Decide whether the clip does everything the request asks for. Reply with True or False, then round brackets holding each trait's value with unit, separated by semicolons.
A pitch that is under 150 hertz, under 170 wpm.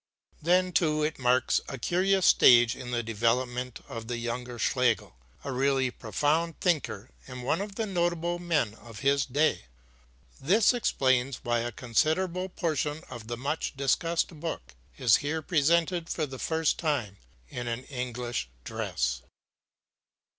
True (135 Hz; 145 wpm)